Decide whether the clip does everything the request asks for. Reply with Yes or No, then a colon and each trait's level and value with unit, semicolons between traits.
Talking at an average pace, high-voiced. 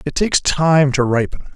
No: average, 195 wpm; medium, 145 Hz